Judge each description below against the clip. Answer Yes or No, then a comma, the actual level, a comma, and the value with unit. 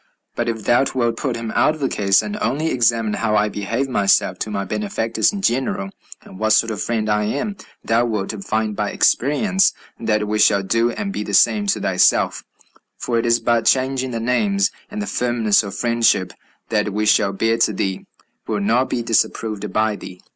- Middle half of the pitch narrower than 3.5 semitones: Yes, average, 2.8 semitones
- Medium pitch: No, low, 115 Hz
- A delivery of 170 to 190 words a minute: No, average, 200 wpm